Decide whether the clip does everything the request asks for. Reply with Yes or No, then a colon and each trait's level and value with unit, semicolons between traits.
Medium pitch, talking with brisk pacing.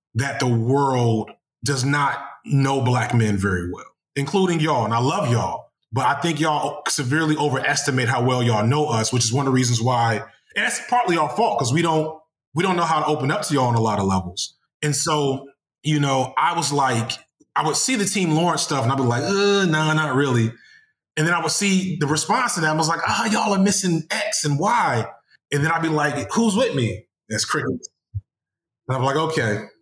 Yes: medium, 145 Hz; fast, 230 wpm